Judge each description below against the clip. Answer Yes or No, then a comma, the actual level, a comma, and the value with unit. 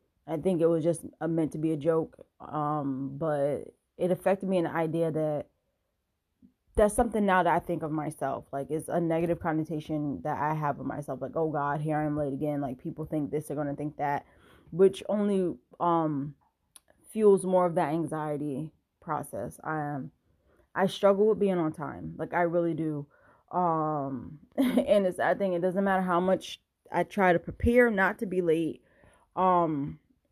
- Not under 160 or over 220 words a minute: Yes, average, 185 wpm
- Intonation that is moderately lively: Yes, average, 3.5 semitones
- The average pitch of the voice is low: No, medium, 160 Hz